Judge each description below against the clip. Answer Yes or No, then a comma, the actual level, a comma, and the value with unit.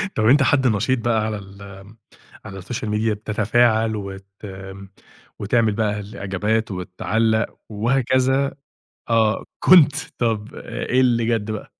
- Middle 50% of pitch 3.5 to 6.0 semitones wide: No, narrow, 2.5 semitones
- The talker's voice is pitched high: No, low, 110 Hz